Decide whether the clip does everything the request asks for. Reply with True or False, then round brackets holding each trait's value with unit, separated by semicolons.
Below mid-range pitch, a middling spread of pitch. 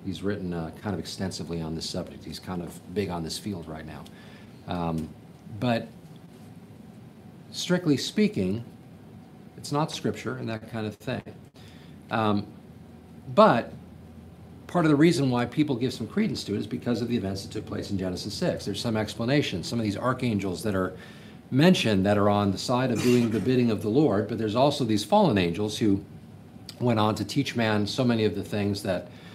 True (105 Hz; 4.4 semitones)